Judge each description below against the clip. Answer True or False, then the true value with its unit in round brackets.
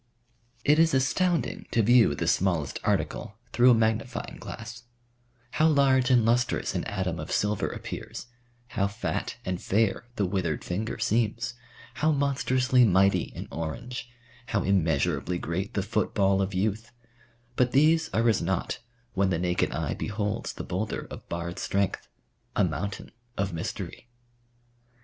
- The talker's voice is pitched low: True (105 Hz)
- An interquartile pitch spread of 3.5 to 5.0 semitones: True (4.7 semitones)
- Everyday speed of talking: True (145 wpm)